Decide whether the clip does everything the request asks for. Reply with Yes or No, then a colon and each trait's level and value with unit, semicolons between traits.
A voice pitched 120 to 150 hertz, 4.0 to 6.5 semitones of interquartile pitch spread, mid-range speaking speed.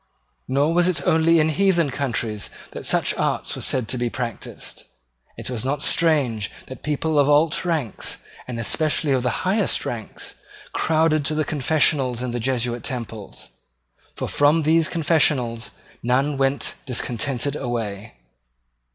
Yes: medium, 140 Hz; average, 4.4 semitones; average, 145 wpm